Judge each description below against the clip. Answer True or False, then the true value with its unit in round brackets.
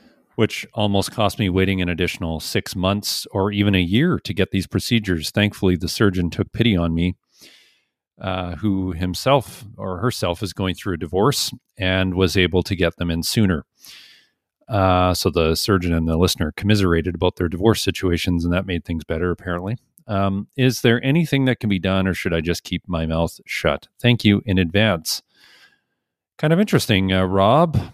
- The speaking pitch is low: True (95 Hz)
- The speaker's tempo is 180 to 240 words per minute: True (185 wpm)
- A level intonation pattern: False (3.0 semitones)